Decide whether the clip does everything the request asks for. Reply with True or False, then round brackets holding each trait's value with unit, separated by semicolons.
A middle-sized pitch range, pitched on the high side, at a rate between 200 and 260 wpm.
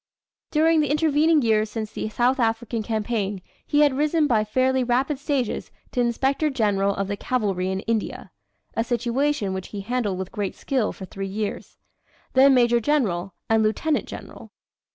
False (4.7 semitones; 235 Hz; 165 wpm)